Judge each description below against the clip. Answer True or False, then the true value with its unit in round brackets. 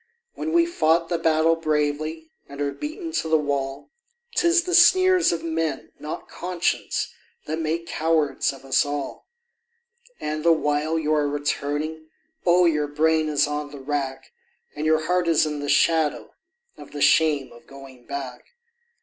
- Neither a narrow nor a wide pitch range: False (2.2 semitones)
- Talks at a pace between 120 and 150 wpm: False (160 wpm)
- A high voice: False (155 Hz)